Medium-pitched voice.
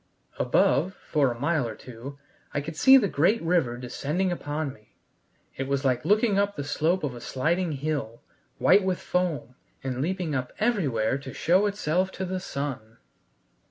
Yes: medium, 150 Hz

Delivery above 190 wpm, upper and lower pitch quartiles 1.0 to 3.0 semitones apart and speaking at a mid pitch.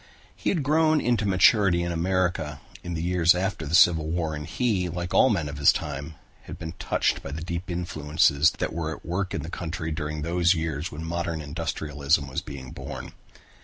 No: average, 200 wpm; average, 2.7 semitones; very low, 85 Hz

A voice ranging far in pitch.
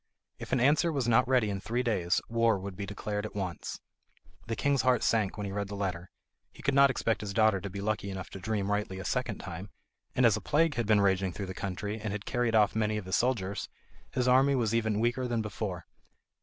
No: average, 3.3 semitones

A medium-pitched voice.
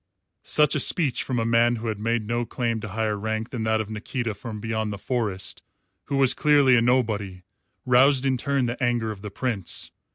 No: low, 115 Hz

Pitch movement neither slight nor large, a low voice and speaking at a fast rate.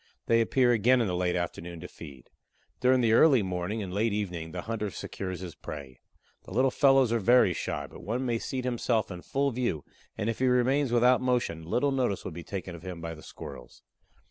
No: wide, 5.9 semitones; low, 110 Hz; fast, 215 wpm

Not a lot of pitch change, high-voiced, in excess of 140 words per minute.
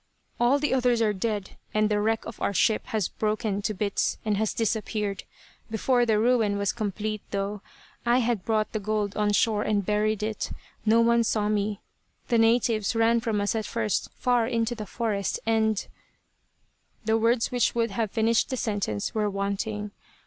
Yes: narrow, 1.9 semitones; high, 215 Hz; average, 185 wpm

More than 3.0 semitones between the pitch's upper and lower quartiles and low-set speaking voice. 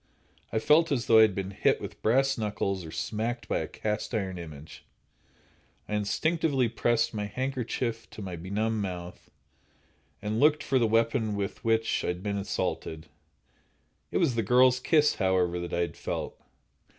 Yes: average, 4.3 semitones; low, 110 Hz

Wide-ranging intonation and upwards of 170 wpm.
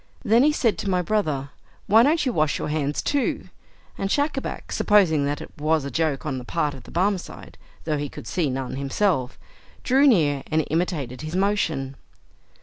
Yes: wide, 6.6 semitones; average, 185 wpm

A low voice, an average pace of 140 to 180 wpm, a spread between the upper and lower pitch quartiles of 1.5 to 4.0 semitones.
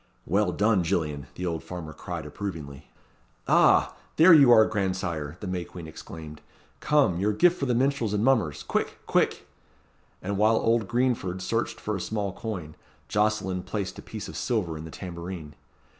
No: very low, 95 Hz; average, 170 wpm; average, 4.8 semitones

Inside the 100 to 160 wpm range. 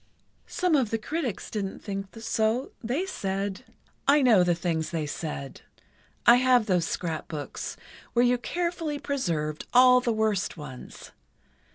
Yes: average, 140 wpm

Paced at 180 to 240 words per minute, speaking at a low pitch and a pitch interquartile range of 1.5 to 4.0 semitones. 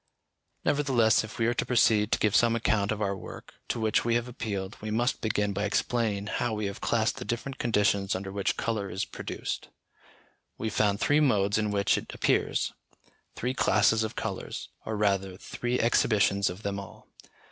Yes: average, 185 wpm; low, 110 Hz; average, 2.7 semitones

